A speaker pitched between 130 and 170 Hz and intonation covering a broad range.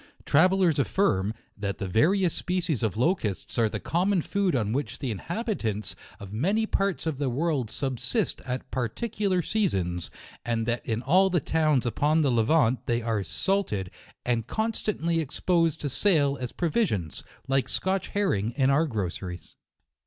Yes: medium, 140 Hz; wide, 8.2 semitones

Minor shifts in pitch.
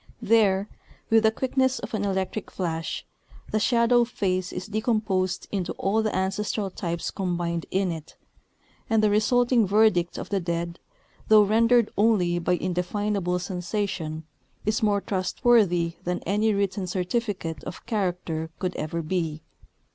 No: average, 3.5 semitones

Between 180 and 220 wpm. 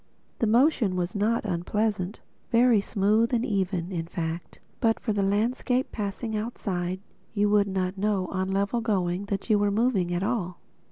No: average, 170 wpm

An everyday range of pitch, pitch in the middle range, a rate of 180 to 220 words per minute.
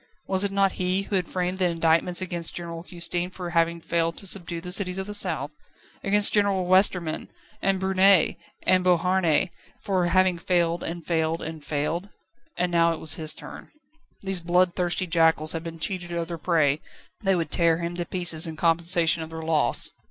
No: narrow, 2.1 semitones; medium, 175 Hz; average, 185 wpm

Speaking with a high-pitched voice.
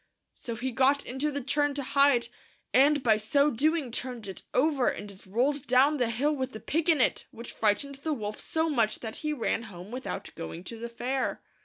Yes: very high, 260 Hz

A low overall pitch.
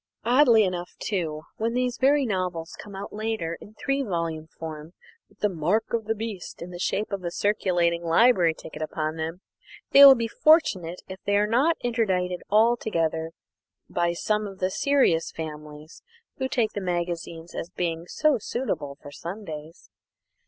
No: medium, 185 Hz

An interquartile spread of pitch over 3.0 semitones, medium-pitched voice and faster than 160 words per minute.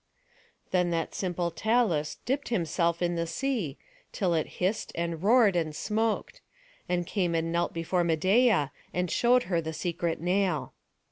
No: average, 3.7 semitones; medium, 175 Hz; average, 150 wpm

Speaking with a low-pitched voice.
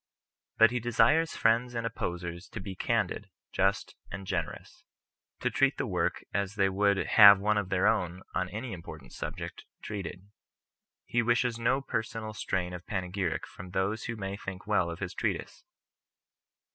Yes: low, 100 Hz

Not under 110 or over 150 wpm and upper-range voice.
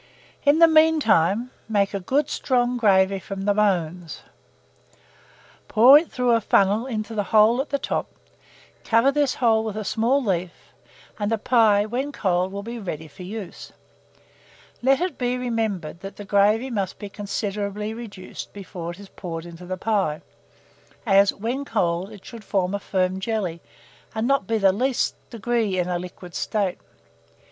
No: average, 170 wpm; high, 210 Hz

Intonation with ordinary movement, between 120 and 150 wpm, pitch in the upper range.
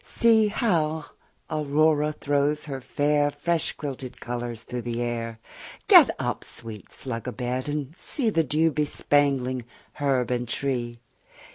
No: average, 3.7 semitones; average, 140 wpm; medium, 140 Hz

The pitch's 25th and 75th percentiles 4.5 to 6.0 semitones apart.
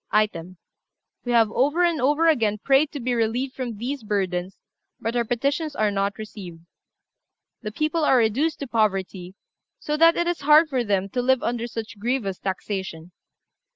Yes: wide, 5.6 semitones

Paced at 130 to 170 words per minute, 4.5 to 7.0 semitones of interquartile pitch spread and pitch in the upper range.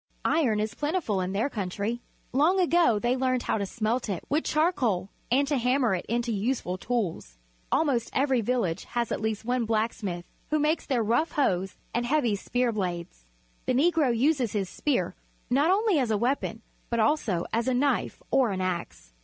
No: average, 185 wpm; average, 5.1 semitones; high, 240 Hz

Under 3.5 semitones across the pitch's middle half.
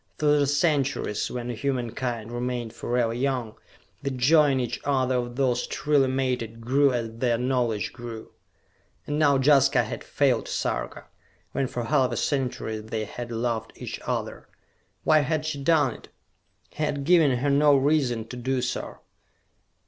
Yes: average, 3.0 semitones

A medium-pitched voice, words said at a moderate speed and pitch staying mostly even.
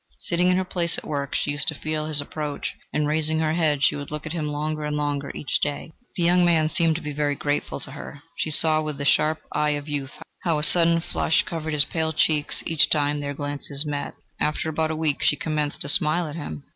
No: medium, 150 Hz; fast, 245 wpm; narrow, 1.6 semitones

